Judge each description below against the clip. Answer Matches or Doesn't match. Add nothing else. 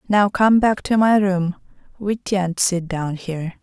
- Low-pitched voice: Doesn't match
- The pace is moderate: Matches